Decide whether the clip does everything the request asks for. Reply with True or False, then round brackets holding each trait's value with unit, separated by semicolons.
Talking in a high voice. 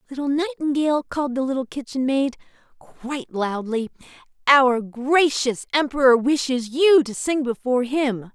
True (265 Hz)